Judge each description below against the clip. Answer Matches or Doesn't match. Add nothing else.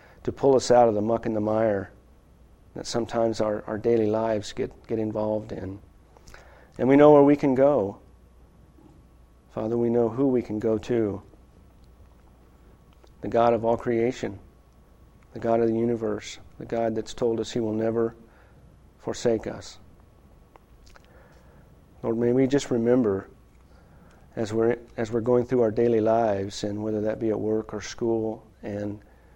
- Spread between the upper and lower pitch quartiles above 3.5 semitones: Doesn't match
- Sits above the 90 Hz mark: Matches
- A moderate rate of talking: Matches